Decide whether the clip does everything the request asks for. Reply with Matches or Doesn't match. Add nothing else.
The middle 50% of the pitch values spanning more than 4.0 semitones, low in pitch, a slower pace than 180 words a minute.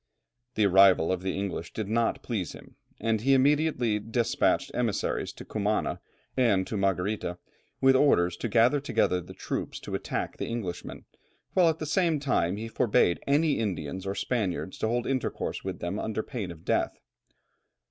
Matches